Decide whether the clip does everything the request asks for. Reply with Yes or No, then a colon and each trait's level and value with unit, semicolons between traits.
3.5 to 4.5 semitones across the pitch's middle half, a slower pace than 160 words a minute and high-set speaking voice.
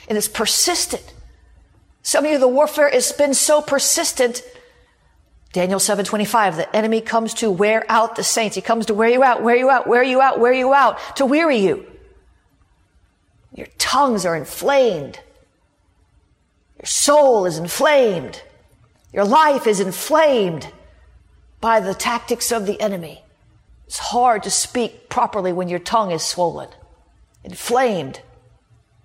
No: wide, 5.4 semitones; average, 145 wpm; high, 230 Hz